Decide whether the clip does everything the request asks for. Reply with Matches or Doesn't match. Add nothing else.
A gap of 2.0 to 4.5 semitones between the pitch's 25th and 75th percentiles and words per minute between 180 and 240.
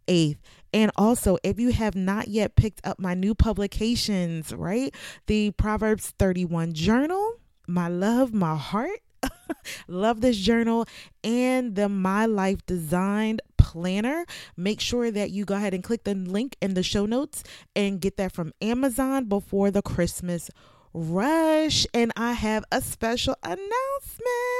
Doesn't match